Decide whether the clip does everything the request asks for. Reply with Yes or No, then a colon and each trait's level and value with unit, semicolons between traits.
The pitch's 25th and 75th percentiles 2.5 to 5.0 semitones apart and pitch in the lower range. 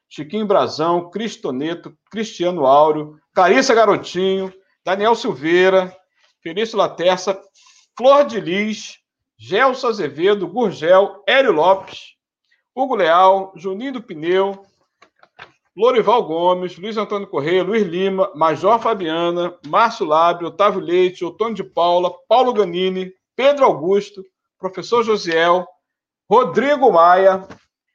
No: average, 3.6 semitones; high, 190 Hz